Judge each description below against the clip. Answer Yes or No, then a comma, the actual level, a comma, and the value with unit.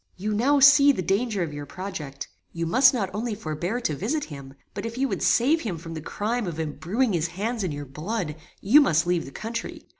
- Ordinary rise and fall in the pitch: No, wide, 6.6 semitones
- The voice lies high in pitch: Yes, high, 195 Hz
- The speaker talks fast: Yes, fast, 220 wpm